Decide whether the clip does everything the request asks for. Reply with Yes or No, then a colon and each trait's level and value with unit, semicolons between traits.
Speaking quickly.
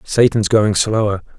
No: slow, 130 wpm